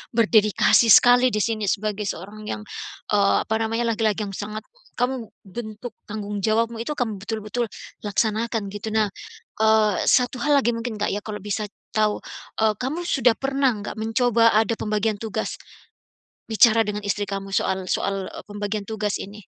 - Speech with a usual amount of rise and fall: No, narrow, 1.9 semitones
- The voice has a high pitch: Yes, high, 215 Hz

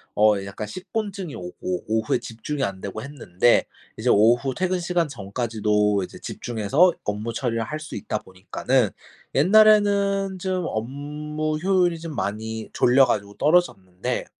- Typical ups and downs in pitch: No, wide, 8.7 semitones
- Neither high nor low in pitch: No, low, 125 Hz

